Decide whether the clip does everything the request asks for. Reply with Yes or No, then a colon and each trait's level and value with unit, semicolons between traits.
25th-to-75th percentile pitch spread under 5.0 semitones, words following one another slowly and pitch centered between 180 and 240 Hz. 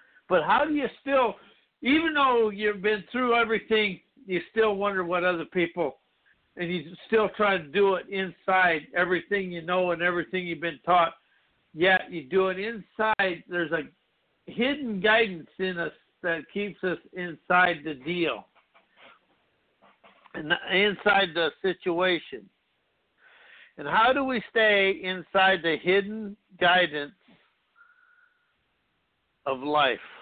Yes: average, 3.7 semitones; slow, 130 wpm; high, 190 Hz